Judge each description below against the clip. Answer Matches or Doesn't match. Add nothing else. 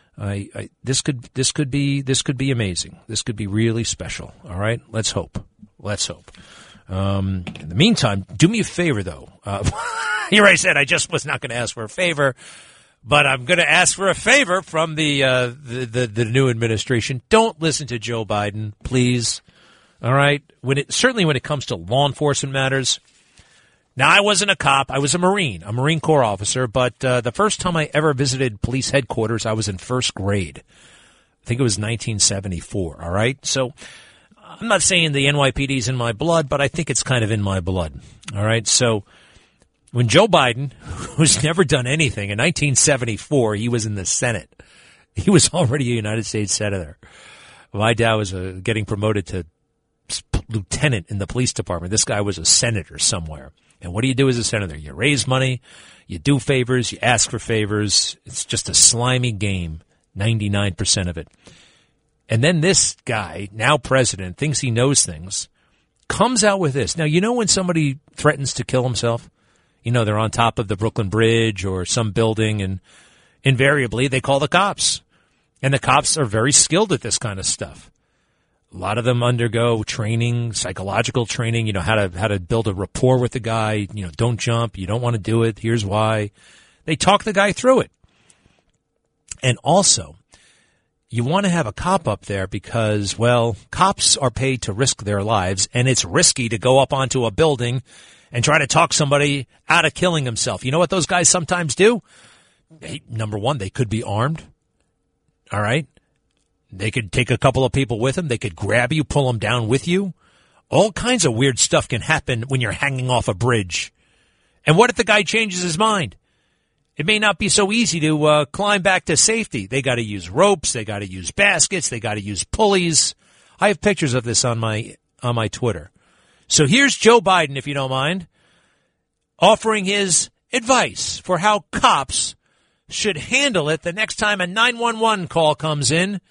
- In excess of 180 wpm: Matches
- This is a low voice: Matches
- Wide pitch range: Matches